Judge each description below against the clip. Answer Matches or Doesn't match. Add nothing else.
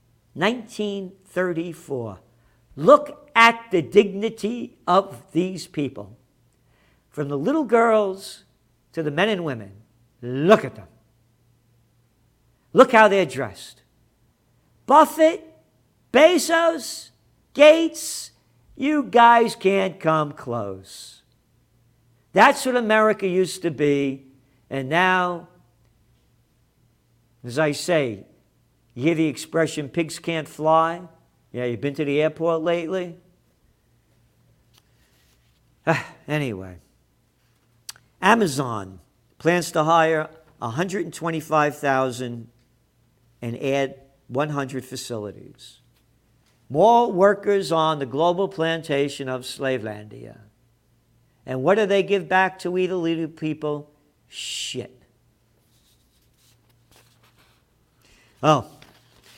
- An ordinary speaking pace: Doesn't match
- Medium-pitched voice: Matches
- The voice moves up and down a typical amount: Doesn't match